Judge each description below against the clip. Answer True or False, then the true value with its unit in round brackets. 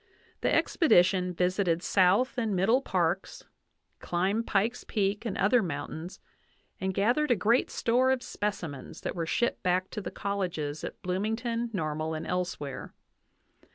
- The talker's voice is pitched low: False (190 Hz)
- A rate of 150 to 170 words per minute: False (140 wpm)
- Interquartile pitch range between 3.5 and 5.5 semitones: True (4.3 semitones)